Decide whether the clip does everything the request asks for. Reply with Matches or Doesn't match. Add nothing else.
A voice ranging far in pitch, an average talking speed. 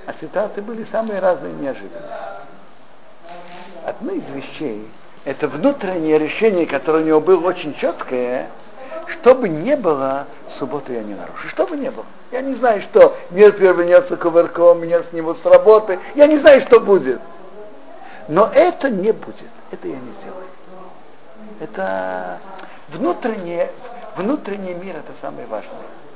Matches